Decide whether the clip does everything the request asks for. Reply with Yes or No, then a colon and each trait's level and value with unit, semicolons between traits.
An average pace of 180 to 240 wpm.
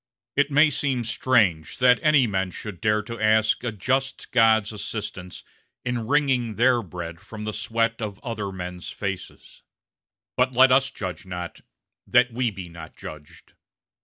No: average, 155 wpm